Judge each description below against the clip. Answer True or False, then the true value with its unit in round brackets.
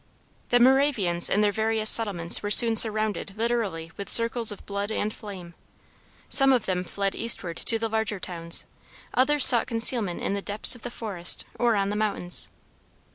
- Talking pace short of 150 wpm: False (175 wpm)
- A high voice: True (215 Hz)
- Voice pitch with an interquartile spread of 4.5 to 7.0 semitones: False (2.9 semitones)